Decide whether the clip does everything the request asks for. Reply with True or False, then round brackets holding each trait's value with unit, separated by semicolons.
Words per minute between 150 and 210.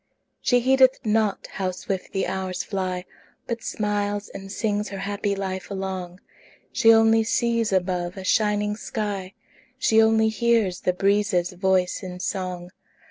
False (140 wpm)